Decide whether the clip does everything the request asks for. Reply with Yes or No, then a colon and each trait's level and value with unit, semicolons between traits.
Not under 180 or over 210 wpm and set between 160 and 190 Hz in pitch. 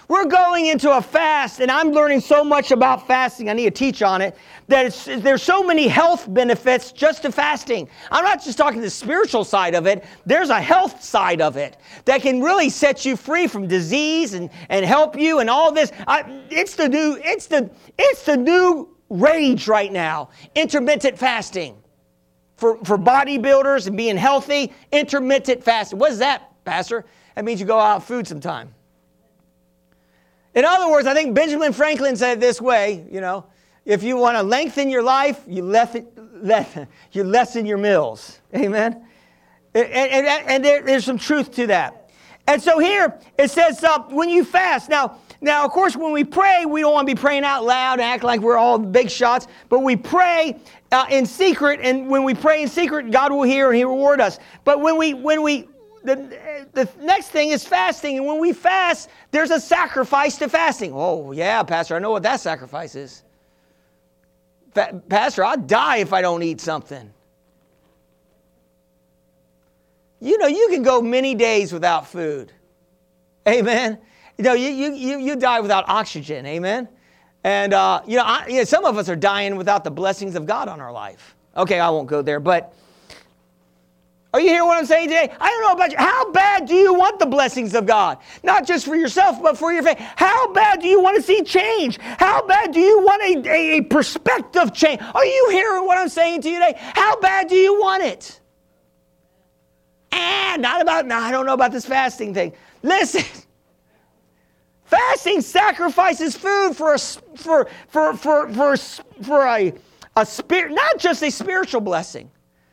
No: average, 190 wpm; very high, 265 Hz